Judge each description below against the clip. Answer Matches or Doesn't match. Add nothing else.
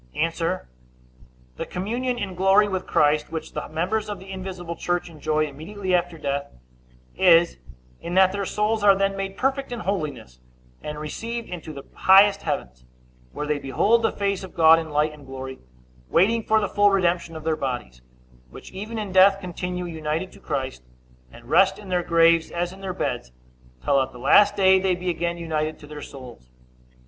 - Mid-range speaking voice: Matches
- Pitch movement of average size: Matches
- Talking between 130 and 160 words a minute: Doesn't match